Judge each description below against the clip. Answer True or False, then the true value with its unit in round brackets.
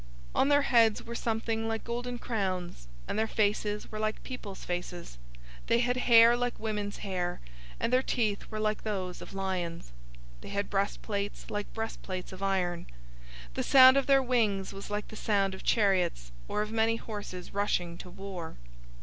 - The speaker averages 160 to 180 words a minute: True (175 wpm)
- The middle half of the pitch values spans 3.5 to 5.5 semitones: False (3.1 semitones)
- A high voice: True (210 Hz)